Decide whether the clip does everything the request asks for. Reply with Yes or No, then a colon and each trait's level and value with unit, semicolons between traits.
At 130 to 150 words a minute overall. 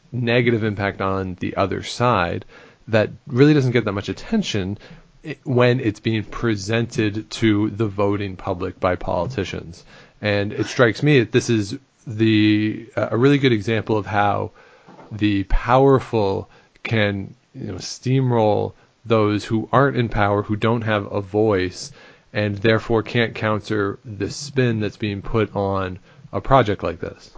Yes: average, 145 wpm